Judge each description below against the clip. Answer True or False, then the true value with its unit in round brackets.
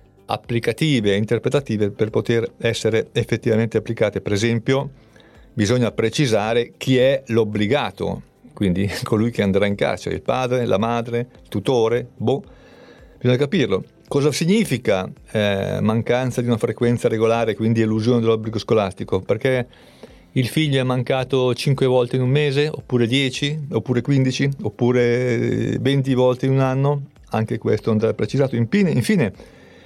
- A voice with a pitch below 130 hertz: True (120 Hz)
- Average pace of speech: True (135 wpm)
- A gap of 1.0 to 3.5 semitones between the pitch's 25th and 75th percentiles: True (3.0 semitones)